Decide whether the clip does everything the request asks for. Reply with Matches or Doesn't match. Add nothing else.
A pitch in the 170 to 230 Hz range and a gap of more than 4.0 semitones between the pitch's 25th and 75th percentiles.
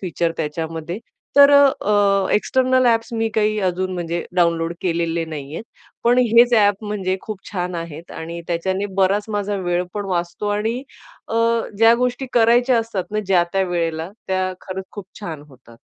Matches